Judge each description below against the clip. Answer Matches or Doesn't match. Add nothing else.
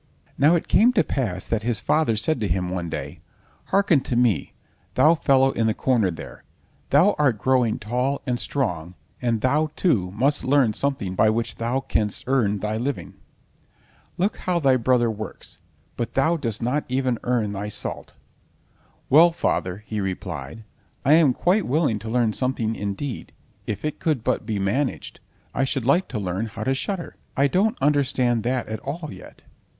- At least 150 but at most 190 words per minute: Matches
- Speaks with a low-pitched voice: Matches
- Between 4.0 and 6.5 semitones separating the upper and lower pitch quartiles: Matches